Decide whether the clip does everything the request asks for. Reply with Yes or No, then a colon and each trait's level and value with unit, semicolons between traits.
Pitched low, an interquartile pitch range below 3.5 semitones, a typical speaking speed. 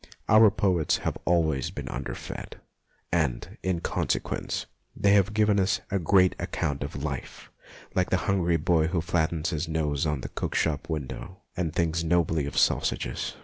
Yes: very low, 85 Hz; average, 2.9 semitones; average, 160 wpm